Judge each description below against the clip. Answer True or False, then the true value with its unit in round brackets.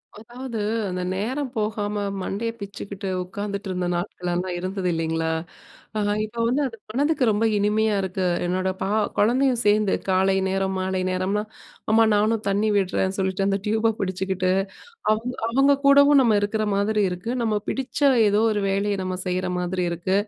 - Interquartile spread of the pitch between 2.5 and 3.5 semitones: True (2.8 semitones)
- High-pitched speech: True (205 Hz)